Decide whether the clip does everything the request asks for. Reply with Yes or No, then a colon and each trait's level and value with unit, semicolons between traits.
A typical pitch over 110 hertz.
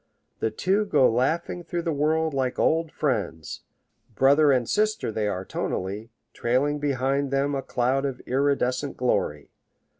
Yes: low, 135 Hz